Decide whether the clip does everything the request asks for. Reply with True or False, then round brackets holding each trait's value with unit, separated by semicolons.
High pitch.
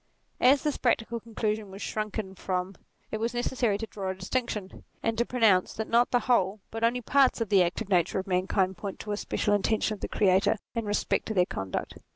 True (215 Hz)